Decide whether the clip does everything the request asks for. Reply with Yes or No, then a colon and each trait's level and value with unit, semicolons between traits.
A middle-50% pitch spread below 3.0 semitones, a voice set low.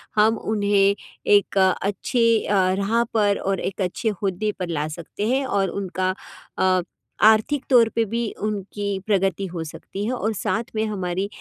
No: narrow, 2.5 semitones; high, 200 Hz